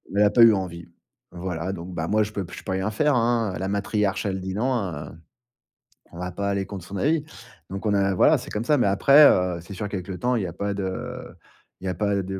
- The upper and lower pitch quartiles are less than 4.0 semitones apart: Yes, narrow, 2.4 semitones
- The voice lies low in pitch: Yes, low, 100 Hz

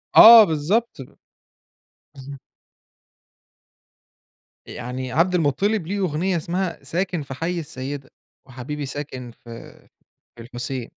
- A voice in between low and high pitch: Yes, medium, 145 Hz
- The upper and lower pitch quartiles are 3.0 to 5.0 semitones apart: No, wide, 5.4 semitones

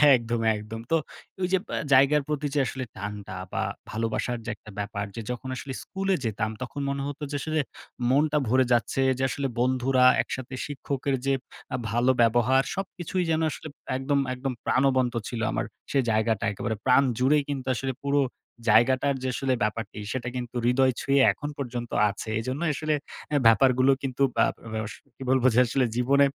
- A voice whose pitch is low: Yes, low, 130 Hz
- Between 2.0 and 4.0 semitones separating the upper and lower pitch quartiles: Yes, average, 2.9 semitones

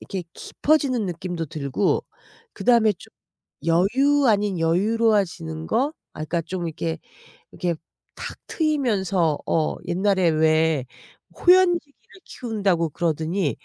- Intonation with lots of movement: Yes, wide, 5.8 semitones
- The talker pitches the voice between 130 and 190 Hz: Yes, medium, 185 Hz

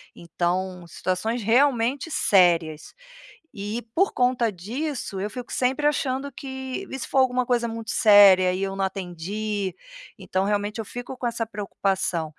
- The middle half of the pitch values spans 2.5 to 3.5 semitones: No, average, 5.0 semitones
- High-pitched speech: Yes, high, 215 Hz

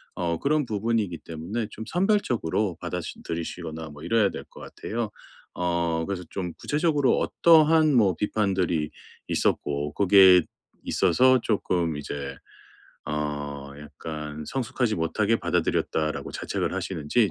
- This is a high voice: No, very low, 90 Hz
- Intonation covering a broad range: Yes, wide, 6.2 semitones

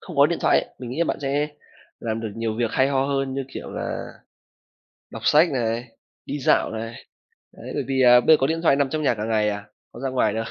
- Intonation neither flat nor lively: Yes, average, 3.8 semitones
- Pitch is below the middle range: Yes, low, 130 Hz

